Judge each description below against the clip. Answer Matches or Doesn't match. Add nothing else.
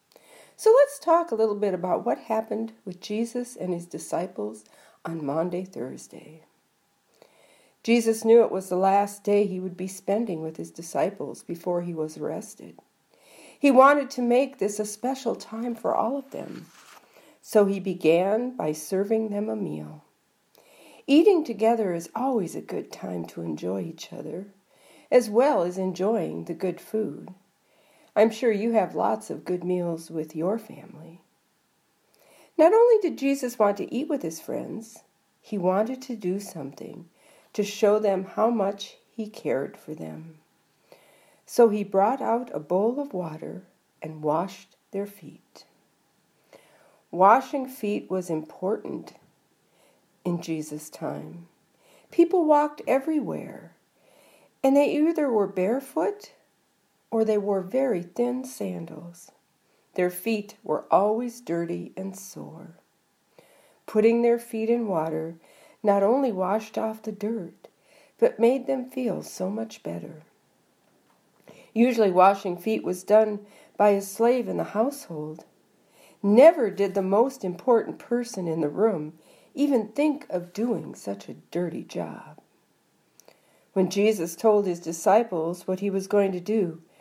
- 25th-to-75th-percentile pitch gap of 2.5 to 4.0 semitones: Doesn't match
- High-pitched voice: Matches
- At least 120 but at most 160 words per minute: Matches